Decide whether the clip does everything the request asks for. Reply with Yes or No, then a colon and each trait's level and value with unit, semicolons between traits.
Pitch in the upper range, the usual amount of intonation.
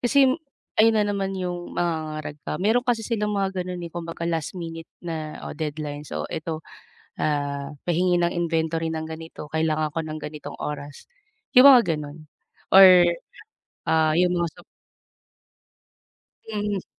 No: medium, 165 Hz; average, 3.4 semitones